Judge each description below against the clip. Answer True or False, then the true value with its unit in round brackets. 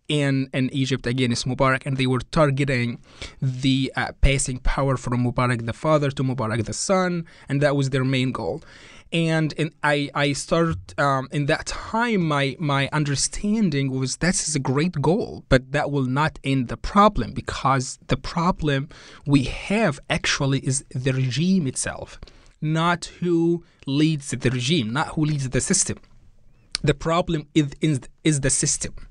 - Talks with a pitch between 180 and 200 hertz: False (140 Hz)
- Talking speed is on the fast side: False (160 wpm)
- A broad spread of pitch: False (3.3 semitones)